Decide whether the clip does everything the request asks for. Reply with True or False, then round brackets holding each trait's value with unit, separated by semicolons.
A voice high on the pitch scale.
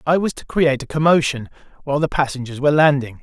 False (145 Hz)